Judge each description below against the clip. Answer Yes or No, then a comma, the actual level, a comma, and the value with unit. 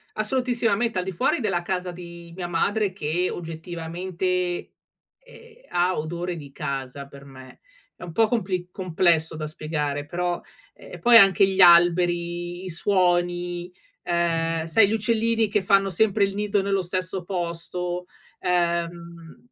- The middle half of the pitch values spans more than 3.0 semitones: No, narrow, 2.4 semitones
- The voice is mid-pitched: Yes, medium, 175 Hz